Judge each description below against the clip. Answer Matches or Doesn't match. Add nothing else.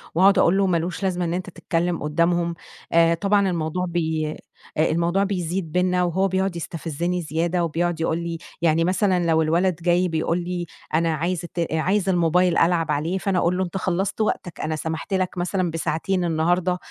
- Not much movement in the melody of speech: Matches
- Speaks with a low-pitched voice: Doesn't match